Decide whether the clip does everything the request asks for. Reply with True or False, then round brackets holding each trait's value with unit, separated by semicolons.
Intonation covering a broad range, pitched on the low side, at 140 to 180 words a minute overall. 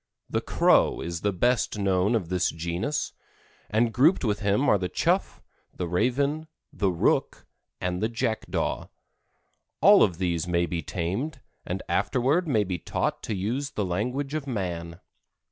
True (5.9 semitones; 100 Hz; 155 wpm)